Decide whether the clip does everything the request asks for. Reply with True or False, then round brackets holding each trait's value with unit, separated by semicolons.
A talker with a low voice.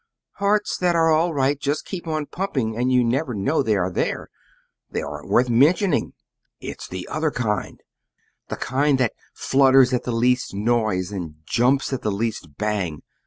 True (125 Hz)